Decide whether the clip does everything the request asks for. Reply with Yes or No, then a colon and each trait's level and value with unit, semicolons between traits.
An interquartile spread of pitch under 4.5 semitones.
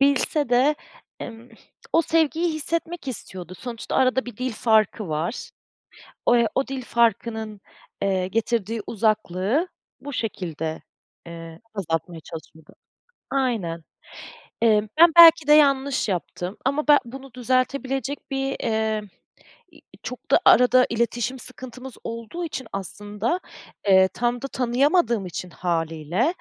No: wide, 5.4 semitones